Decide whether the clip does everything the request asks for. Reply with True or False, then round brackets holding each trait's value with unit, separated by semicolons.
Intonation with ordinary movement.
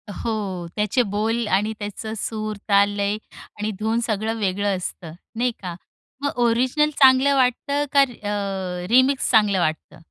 True (3.6 semitones)